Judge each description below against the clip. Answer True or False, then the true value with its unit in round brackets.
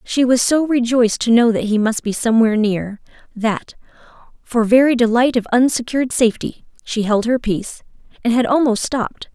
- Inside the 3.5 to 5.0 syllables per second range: False (5.5 syllables/s)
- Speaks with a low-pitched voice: False (235 Hz)